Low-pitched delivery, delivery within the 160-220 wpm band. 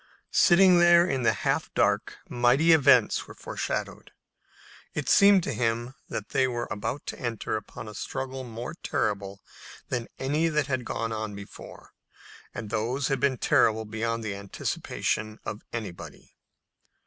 No: low, 120 Hz; average, 145 wpm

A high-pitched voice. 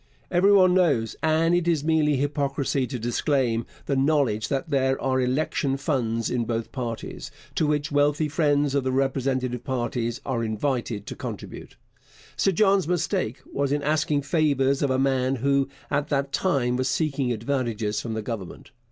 No: low, 135 Hz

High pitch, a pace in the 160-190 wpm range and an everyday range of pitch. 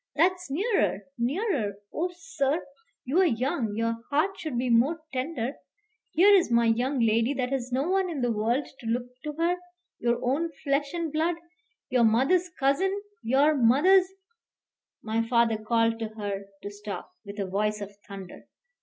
No: very high, 255 Hz; average, 165 wpm; wide, 6.0 semitones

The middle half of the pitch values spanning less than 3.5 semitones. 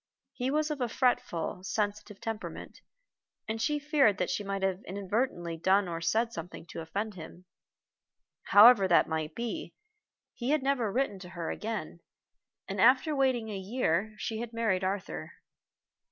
No: average, 4.8 semitones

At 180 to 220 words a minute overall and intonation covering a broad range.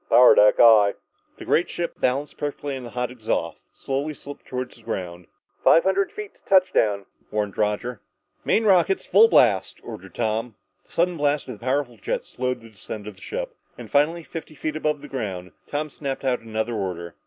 Yes: average, 190 wpm; wide, 6.1 semitones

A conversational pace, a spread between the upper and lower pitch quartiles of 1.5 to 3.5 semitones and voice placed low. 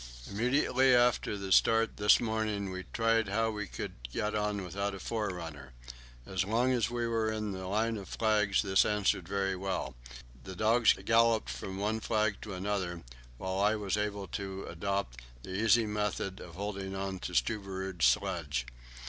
Yes: average, 165 wpm; narrow, 2.6 semitones; low, 100 Hz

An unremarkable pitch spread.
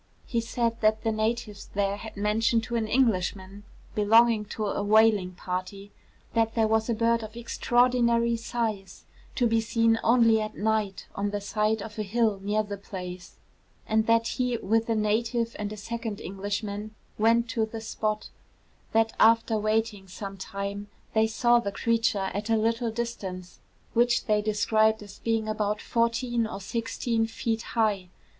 No: narrow, 1.9 semitones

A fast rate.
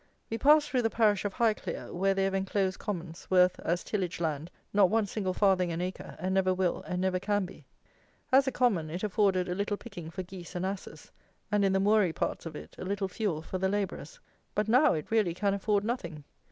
Yes: fast, 220 wpm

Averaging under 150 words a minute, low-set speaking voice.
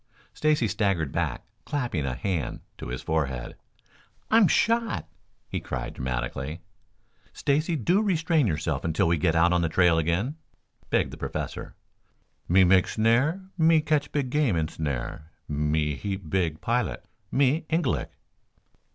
Yes: average, 140 wpm; very low, 95 Hz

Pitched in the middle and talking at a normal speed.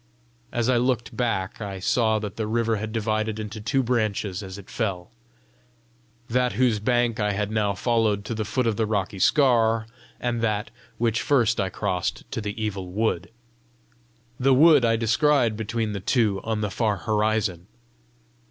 No: low, 110 Hz; average, 170 wpm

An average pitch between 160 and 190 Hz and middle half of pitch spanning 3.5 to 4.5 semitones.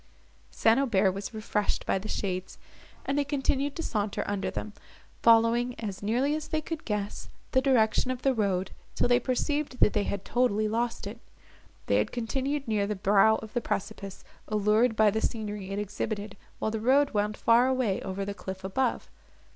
No: high, 220 Hz; average, 3.9 semitones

